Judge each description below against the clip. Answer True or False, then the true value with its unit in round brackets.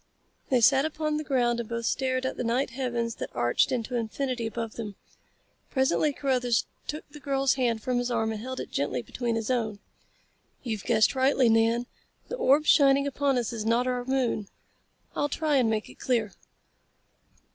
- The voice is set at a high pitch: True (245 Hz)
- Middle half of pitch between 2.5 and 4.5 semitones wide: True (2.9 semitones)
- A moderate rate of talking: True (185 wpm)